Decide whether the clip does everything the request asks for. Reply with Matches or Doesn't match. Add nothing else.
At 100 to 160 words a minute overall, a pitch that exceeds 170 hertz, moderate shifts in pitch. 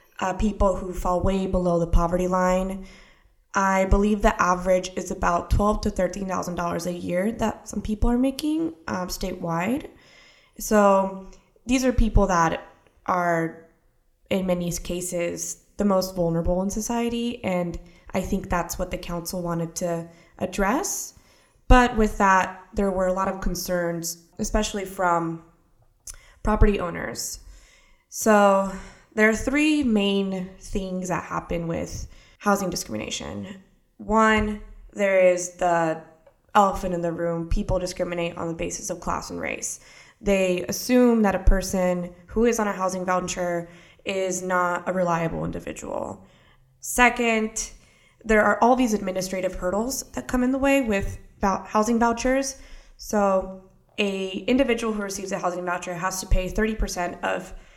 Matches